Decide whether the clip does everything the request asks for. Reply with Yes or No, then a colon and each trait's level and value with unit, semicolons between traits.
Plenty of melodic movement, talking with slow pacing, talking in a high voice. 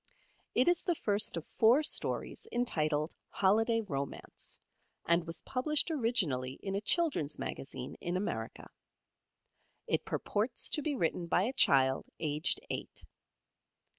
Yes: wide, 8.4 semitones; slow, 130 wpm; high, 195 Hz